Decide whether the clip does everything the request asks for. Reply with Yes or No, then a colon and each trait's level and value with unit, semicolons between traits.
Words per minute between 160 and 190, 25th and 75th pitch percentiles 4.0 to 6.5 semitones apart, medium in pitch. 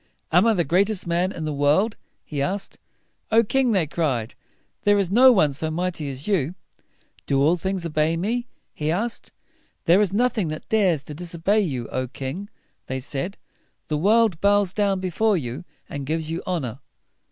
Yes: average, 180 wpm; average, 5.1 semitones; medium, 175 Hz